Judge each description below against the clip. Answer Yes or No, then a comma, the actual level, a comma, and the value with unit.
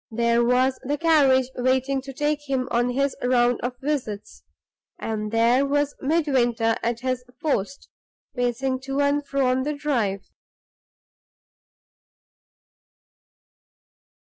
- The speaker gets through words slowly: Yes, slow, 115 wpm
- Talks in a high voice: Yes, very high, 260 Hz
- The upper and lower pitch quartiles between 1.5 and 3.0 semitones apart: Yes, average, 2.7 semitones